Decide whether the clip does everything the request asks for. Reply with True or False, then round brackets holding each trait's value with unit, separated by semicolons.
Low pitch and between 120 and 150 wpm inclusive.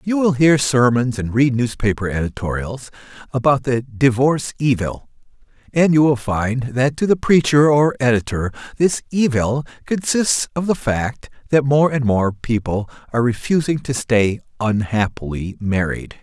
True (125 Hz; 145 wpm)